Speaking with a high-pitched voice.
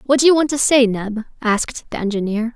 Yes: high, 240 Hz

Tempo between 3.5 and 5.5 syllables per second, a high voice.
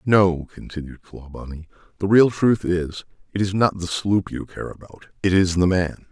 No: 4.8 syllables/s; very low, 95 Hz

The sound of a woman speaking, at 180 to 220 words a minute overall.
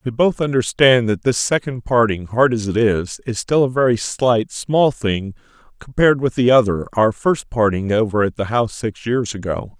No: male; average, 195 wpm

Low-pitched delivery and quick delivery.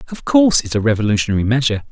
Yes: low, 125 Hz; fast, 220 wpm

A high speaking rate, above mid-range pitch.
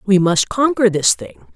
No: average, 195 wpm; high, 205 Hz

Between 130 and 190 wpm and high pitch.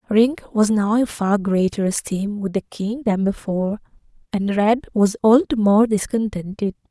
Yes: average, 165 wpm; high, 210 Hz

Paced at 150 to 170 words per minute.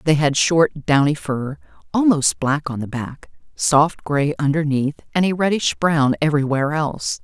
Yes: average, 160 wpm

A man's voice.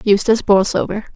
No: female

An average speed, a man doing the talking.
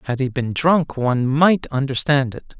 Yes: average, 185 wpm; male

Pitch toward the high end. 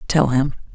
No: medium, 140 Hz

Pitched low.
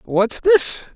No: medium, 185 Hz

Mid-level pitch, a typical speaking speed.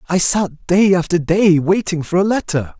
Yes: medium, 180 Hz; average, 195 wpm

